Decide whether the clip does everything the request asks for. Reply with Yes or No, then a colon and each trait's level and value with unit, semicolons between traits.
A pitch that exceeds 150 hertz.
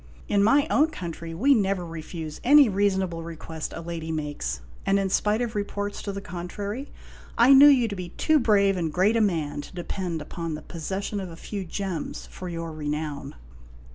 Yes: medium, 185 Hz